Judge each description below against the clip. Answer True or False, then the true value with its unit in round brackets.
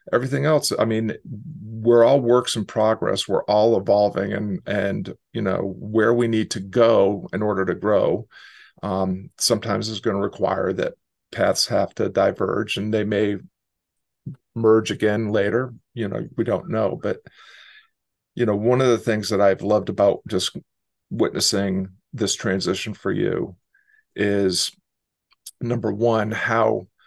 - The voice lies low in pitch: True (110 Hz)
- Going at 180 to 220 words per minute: False (150 wpm)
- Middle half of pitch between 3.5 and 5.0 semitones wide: False (2.7 semitones)